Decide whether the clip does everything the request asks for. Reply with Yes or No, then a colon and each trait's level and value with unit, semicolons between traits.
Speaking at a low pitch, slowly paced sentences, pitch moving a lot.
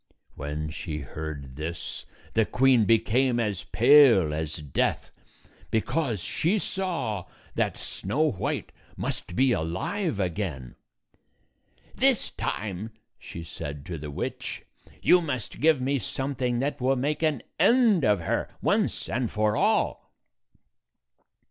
Yes: low, 110 Hz; slow, 125 wpm; wide, 8.6 semitones